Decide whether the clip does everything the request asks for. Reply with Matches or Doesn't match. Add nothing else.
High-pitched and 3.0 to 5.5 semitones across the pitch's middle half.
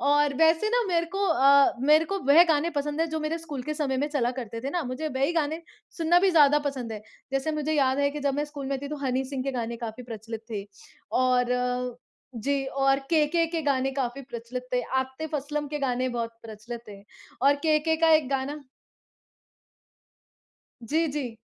Matches